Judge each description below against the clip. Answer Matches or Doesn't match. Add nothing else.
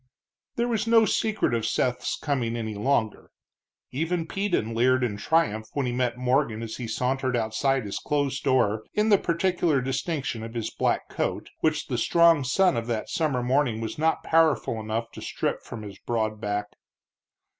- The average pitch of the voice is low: Matches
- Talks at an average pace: Matches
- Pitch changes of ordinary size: Doesn't match